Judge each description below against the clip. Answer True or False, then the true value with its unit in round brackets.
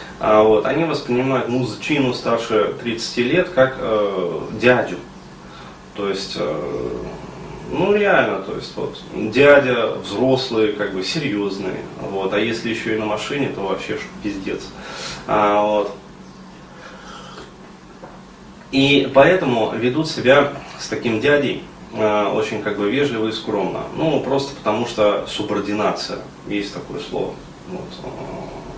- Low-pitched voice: True (115 Hz)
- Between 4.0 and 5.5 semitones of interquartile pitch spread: True (5.1 semitones)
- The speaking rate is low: False (125 wpm)